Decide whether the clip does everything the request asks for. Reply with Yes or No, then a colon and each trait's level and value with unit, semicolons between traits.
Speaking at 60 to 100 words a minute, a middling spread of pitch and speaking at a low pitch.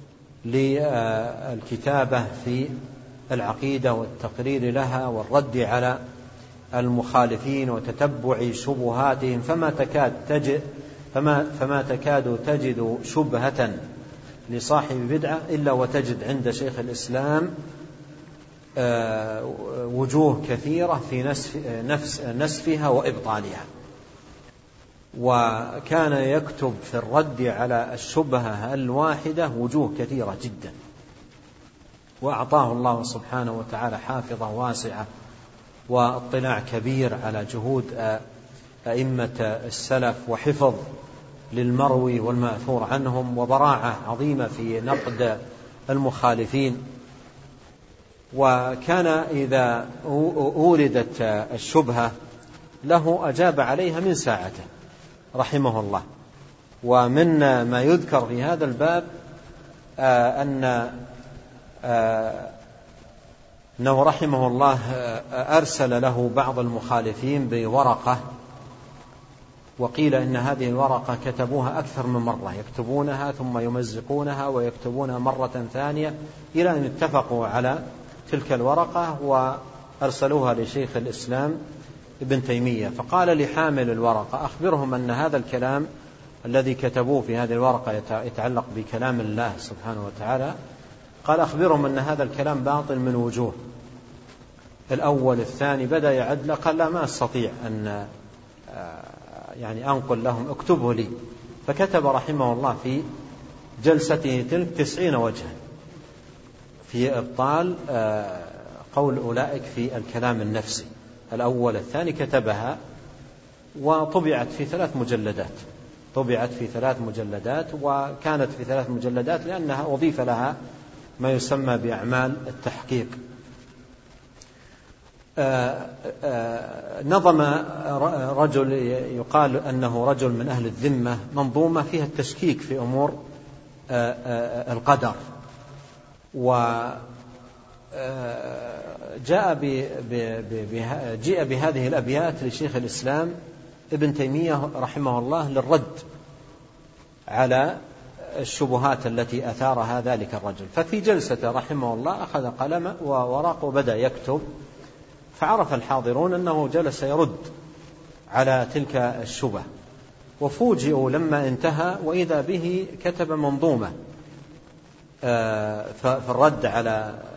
Yes: average, 90 wpm; average, 3.2 semitones; low, 130 Hz